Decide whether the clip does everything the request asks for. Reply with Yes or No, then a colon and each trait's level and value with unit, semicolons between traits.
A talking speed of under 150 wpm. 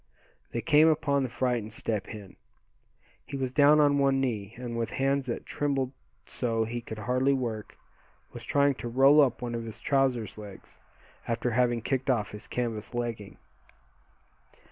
No: average, 165 wpm